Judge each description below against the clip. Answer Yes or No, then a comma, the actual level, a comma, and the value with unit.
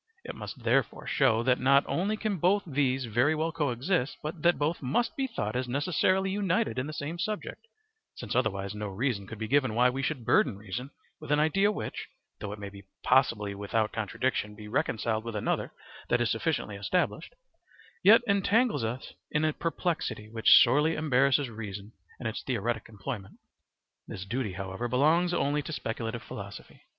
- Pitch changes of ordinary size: No, wide, 6.4 semitones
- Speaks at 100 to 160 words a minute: No, average, 175 wpm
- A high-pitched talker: No, low, 130 Hz